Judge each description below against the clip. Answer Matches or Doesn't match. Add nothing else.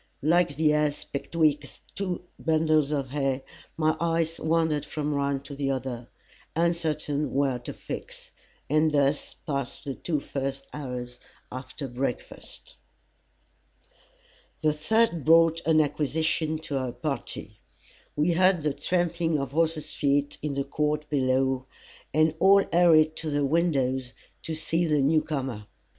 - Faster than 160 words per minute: Doesn't match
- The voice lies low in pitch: Doesn't match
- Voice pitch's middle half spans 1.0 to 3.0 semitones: Matches